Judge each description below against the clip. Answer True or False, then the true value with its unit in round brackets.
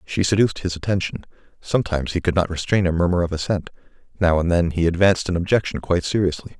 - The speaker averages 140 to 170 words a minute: False (200 wpm)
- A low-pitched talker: True (90 Hz)